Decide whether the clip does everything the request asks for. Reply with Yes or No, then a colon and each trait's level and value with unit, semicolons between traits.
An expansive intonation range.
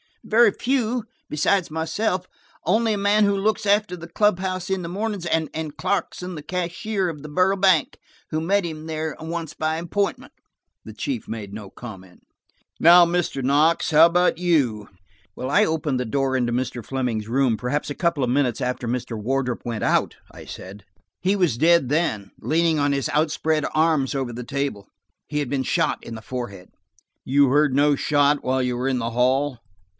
Yes: wide, 5.8 semitones